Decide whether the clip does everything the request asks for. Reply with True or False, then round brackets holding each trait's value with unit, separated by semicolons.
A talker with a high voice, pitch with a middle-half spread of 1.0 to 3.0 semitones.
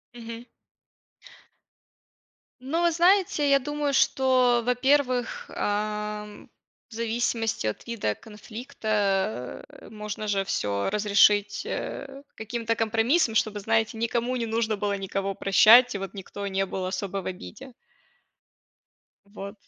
False (220 Hz; 3.5 semitones)